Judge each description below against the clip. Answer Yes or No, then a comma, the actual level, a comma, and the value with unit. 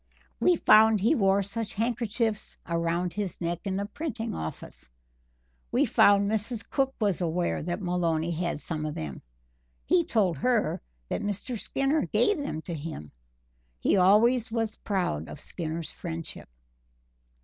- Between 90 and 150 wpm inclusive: Yes, average, 145 wpm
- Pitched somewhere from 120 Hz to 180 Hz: No, high, 195 Hz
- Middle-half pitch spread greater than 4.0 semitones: Yes, average, 5.1 semitones